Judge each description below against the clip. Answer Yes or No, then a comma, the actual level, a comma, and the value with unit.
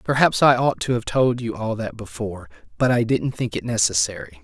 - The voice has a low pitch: Yes, low, 115 Hz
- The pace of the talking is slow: No, fast, 205 wpm